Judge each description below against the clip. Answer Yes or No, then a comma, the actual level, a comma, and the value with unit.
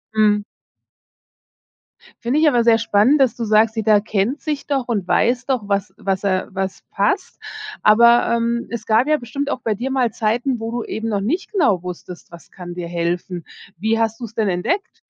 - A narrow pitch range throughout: No, average, 3.5 semitones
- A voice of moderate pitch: No, high, 225 Hz